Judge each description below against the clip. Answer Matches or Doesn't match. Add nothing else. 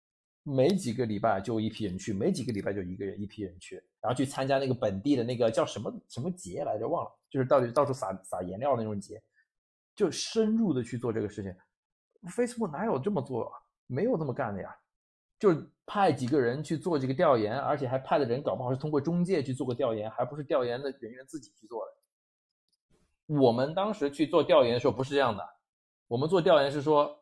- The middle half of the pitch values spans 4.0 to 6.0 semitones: Matches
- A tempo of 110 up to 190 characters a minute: Doesn't match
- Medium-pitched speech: Doesn't match